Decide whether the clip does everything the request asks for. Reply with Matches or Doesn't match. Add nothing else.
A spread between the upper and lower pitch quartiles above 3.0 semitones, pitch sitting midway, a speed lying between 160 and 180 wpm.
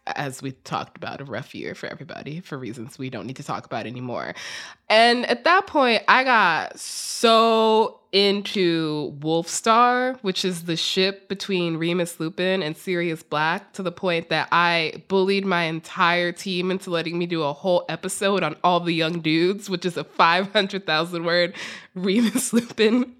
Matches